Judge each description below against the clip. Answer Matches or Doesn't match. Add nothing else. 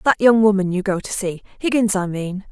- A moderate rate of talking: Doesn't match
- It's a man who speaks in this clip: Doesn't match